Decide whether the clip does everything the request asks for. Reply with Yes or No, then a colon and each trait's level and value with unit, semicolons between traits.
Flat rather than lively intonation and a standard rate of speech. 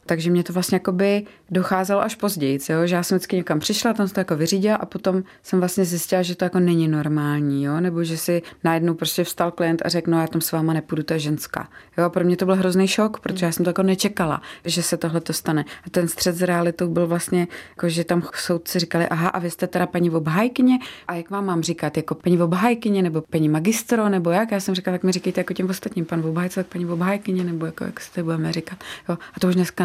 No: narrow, 2.0 semitones; fast, 245 wpm